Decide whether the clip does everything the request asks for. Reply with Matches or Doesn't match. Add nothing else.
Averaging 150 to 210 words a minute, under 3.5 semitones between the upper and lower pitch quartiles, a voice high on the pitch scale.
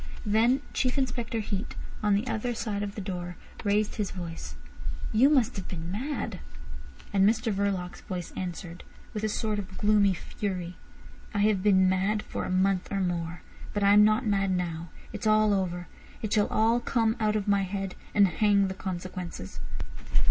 Matches